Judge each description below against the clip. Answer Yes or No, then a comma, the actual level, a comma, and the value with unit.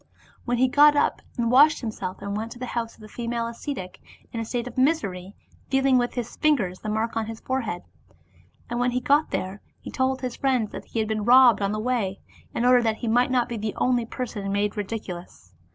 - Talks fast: Yes, fast, 225 wpm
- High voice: Yes, high, 235 Hz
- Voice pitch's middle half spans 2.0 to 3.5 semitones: Yes, average, 3.0 semitones